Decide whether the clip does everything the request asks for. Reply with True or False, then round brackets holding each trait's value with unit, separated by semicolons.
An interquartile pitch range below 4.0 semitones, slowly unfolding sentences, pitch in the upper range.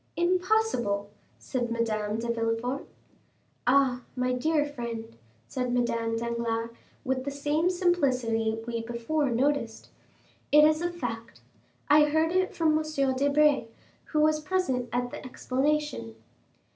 False (4.7 semitones; 125 wpm; 255 Hz)